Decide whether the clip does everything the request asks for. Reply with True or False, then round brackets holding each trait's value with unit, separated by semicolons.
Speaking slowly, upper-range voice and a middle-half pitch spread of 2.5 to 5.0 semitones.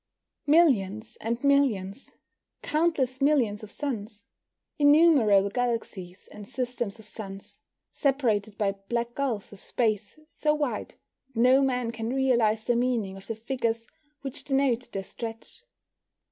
True (130 wpm; 235 Hz; 4.3 semitones)